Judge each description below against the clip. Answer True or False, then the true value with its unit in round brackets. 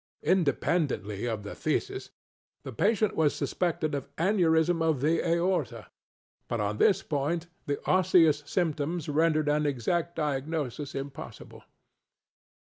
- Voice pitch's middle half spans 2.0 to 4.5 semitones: True (3.5 semitones)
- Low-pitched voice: False (155 Hz)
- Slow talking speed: True (120 wpm)